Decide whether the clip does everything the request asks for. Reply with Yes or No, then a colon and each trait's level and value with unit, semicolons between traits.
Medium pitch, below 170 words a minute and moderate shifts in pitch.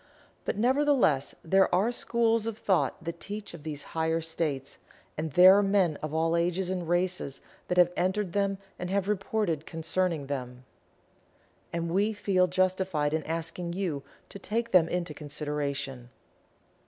Yes: medium, 175 Hz; average, 155 wpm; average, 3.7 semitones